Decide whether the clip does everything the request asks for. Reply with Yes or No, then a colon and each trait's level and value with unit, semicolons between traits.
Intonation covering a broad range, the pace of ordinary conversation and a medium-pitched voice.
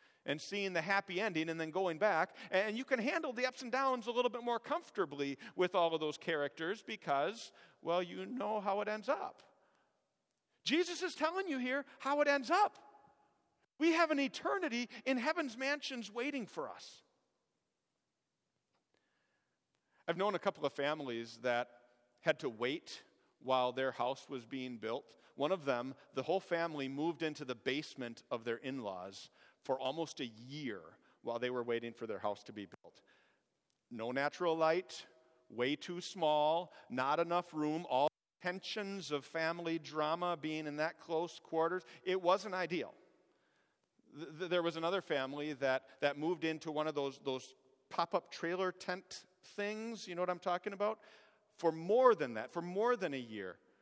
Yes: wide, 7.0 semitones; average, 170 wpm; medium, 170 Hz